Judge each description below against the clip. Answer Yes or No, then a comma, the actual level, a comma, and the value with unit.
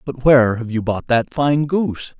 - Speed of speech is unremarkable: No, fast, 220 wpm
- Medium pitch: No, low, 130 Hz